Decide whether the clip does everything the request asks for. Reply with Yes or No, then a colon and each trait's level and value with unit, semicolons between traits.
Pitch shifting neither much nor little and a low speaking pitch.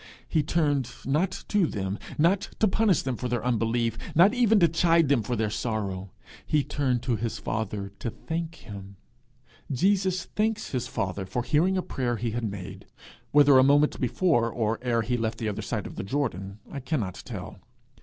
No: wide, 6.6 semitones; low, 125 Hz